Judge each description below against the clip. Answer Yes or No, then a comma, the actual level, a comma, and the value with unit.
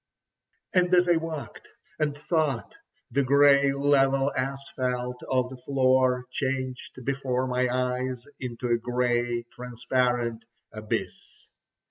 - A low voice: Yes, low, 130 Hz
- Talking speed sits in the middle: No, slow, 110 wpm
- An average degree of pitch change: No, narrow, 1.9 semitones